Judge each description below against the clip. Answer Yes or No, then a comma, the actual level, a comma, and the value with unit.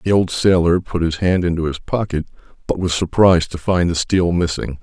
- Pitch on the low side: Yes, very low, 85 Hz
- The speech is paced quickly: Yes, fast, 210 wpm